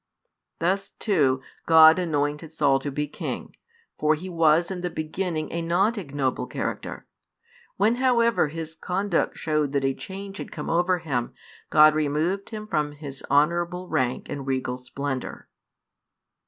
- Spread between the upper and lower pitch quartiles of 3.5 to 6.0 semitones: Yes, average, 3.9 semitones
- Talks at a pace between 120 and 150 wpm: Yes, average, 145 wpm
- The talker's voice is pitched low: No, medium, 160 Hz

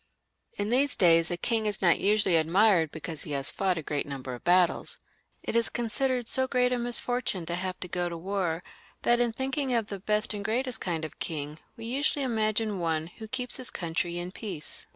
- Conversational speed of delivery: No, fast, 210 wpm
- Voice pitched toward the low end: No, high, 200 Hz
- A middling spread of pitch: No, wide, 6.0 semitones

